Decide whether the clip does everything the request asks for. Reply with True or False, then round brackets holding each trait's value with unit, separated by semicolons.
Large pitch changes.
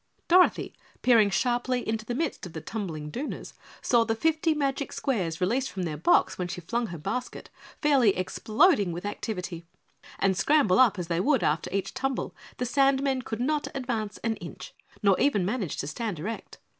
True (6.3 semitones)